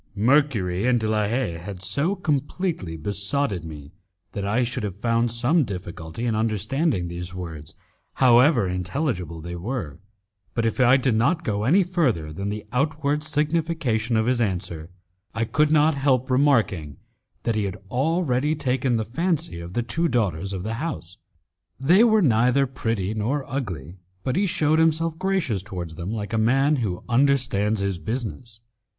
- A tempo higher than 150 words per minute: Yes, average, 165 wpm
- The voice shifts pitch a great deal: Yes, wide, 6.6 semitones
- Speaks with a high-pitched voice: No, low, 115 Hz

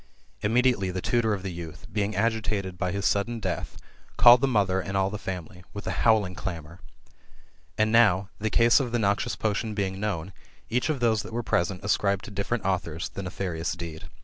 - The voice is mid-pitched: No, low, 100 Hz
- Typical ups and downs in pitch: Yes, average, 3.2 semitones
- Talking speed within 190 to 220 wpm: Yes, average, 200 wpm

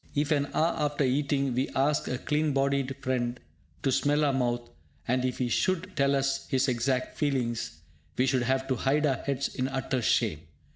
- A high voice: No, low, 135 Hz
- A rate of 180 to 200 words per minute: Yes, average, 190 wpm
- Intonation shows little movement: Yes, narrow, 2.0 semitones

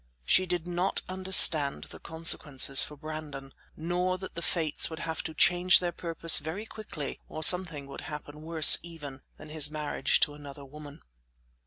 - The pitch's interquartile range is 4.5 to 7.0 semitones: No, average, 3.1 semitones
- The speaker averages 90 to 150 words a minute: No, average, 165 wpm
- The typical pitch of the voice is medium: Yes, medium, 160 Hz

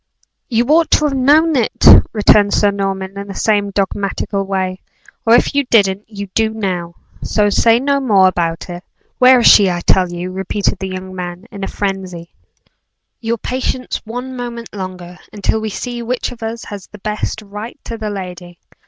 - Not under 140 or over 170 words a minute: No, average, 185 wpm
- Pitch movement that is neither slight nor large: Yes, average, 3.7 semitones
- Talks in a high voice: Yes, high, 205 Hz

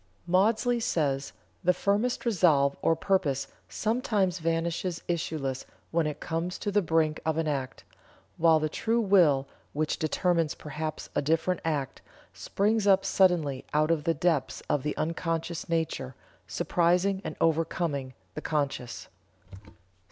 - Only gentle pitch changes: No, average, 3.4 semitones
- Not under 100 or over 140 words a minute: Yes, slow, 135 wpm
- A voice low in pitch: No, medium, 165 Hz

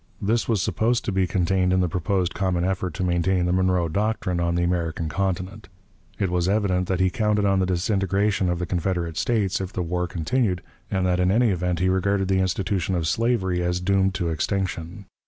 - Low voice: Yes, very low, 95 Hz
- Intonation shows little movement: Yes, narrow, 1.8 semitones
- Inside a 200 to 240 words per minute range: Yes, fast, 205 wpm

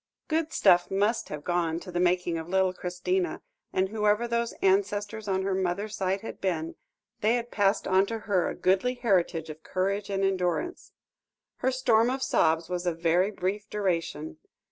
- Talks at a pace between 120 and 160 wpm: No, average, 175 wpm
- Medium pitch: No, high, 195 Hz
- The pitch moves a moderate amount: Yes, average, 3.3 semitones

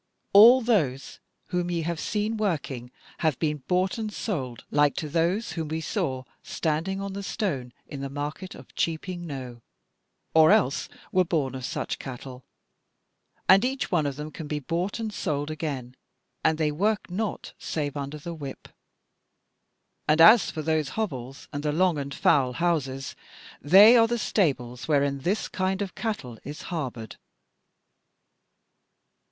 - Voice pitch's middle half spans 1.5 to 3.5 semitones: No, average, 5.2 semitones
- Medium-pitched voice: Yes, medium, 155 Hz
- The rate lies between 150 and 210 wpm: Yes, average, 155 wpm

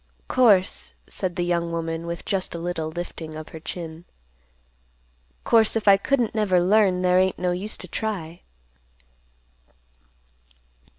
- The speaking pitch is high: No, medium, 180 Hz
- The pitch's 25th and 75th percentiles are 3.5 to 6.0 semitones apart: No, average, 3.1 semitones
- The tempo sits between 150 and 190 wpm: No, slow, 135 wpm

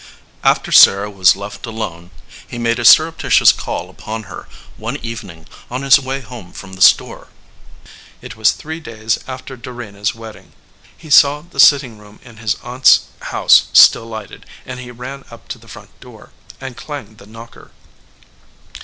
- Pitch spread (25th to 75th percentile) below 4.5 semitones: Yes, average, 3.7 semitones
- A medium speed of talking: Yes, average, 170 wpm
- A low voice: Yes, low, 115 Hz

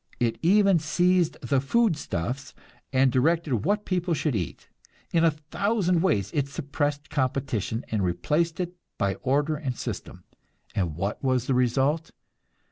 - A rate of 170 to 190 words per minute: No, average, 140 wpm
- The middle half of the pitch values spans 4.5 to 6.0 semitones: Yes, average, 5.1 semitones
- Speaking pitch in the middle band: Yes, medium, 145 Hz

